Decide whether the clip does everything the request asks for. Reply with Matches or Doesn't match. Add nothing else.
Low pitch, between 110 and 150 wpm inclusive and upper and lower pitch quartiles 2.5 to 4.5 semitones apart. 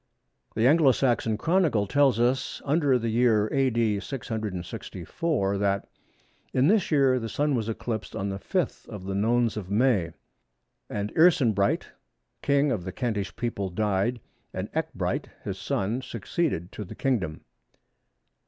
Doesn't match